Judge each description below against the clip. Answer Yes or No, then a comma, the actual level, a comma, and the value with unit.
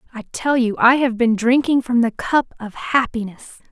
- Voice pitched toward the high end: Yes, high, 240 Hz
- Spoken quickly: No, average, 195 wpm